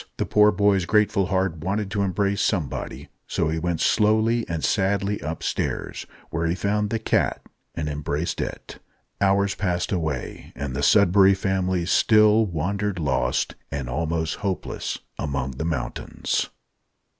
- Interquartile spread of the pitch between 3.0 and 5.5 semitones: Yes, average, 4.3 semitones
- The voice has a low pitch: Yes, very low, 95 Hz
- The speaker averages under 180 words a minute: Yes, average, 140 wpm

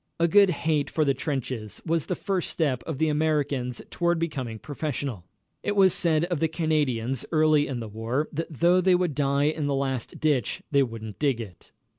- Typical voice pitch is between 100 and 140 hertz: No, medium, 150 Hz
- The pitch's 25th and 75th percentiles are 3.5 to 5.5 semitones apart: Yes, average, 4.0 semitones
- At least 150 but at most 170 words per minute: No, average, 195 wpm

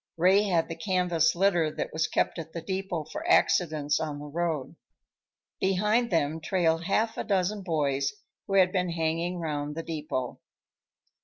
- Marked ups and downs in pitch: No, average, 3.2 semitones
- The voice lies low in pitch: No, medium, 170 Hz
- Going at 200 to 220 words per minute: No, average, 160 wpm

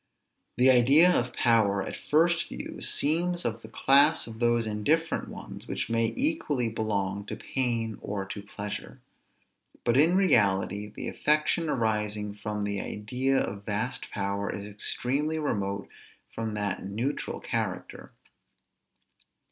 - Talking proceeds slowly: Yes, slow, 130 wpm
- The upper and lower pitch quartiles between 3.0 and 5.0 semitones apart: No, wide, 5.6 semitones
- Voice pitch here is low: Yes, low, 115 Hz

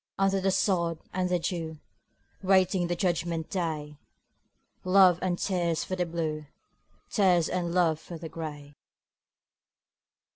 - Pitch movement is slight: Yes, narrow, 2.3 semitones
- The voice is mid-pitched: Yes, medium, 175 Hz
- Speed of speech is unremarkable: No, slow, 125 wpm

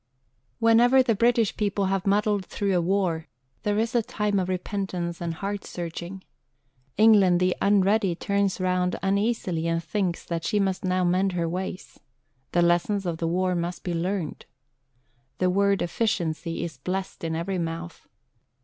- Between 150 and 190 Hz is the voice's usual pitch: Yes, medium, 185 Hz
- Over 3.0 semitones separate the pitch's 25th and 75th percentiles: No, average, 2.7 semitones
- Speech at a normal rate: Yes, average, 160 wpm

